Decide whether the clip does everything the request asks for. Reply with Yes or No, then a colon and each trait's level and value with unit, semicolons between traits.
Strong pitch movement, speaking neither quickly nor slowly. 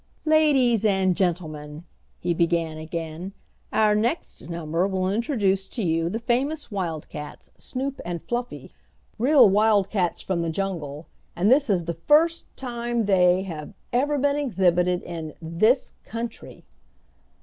No: wide, 6.0 semitones; slow, 130 wpm